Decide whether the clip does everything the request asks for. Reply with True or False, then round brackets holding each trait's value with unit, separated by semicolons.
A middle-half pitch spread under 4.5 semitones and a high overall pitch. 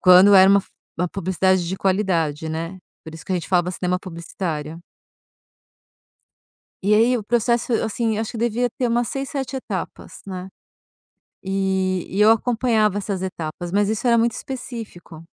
True (4.0 semitones; 195 Hz)